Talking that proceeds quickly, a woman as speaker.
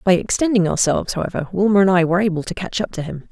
Yes: fast, 255 wpm; female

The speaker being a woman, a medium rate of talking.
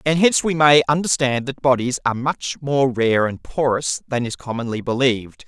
No: male; average, 185 wpm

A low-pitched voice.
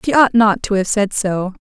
No: high, 210 Hz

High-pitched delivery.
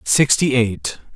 No: low, 130 Hz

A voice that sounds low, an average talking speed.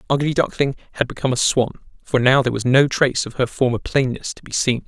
No: low, 130 Hz; fast, 245 wpm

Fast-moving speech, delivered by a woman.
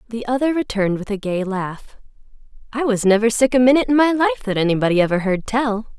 Yes: fast, 210 wpm; female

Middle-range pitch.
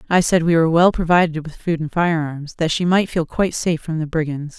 Yes: medium, 165 Hz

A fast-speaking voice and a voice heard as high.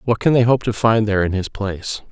No: fast, 285 wpm; low, 110 Hz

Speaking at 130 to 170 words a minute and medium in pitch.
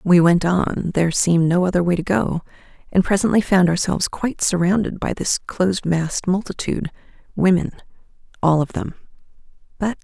Yes: average, 145 wpm; medium, 180 Hz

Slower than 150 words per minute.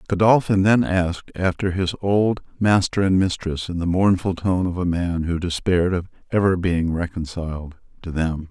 No: average, 170 wpm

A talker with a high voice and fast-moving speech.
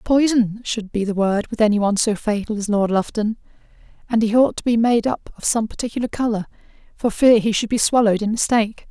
Yes: high, 220 Hz; fast, 215 wpm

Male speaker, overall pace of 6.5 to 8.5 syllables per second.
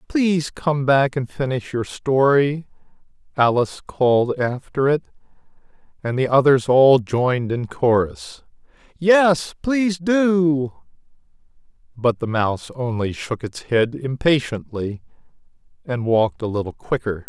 No: male; 4.1 syllables/s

